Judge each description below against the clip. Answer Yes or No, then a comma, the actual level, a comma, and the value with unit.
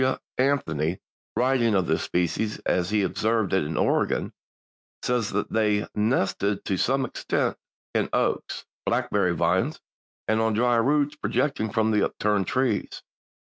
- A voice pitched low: Yes, low, 110 Hz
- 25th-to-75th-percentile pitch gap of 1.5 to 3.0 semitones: No, average, 4.1 semitones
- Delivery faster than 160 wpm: No, slow, 135 wpm